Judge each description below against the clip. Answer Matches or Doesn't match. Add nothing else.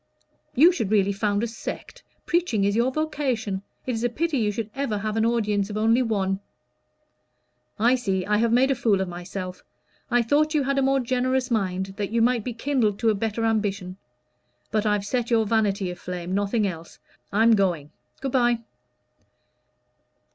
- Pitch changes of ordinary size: Matches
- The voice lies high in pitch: Matches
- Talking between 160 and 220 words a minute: Matches